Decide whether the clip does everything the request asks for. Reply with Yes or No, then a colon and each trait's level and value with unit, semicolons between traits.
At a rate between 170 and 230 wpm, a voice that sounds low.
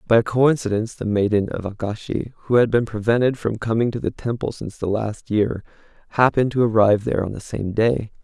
Yes: fast, 205 wpm; low, 110 Hz